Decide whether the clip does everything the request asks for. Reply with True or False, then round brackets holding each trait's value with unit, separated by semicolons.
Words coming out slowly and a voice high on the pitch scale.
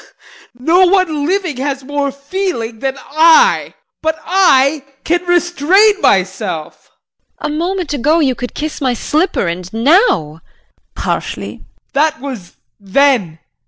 True (125 wpm; 290 Hz)